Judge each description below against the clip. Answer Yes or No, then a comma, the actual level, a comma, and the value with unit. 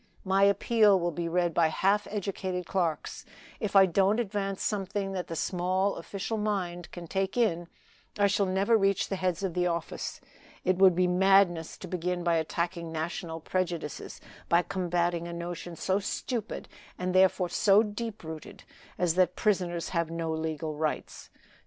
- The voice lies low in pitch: No, medium, 180 Hz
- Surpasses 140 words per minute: Yes, average, 165 wpm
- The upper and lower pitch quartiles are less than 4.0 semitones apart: Yes, narrow, 2.4 semitones